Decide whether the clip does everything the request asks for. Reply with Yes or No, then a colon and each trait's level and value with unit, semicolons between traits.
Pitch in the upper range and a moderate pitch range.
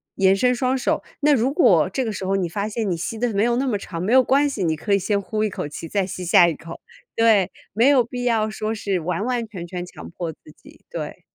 Yes: high, 210 Hz; average, 4.8 semitones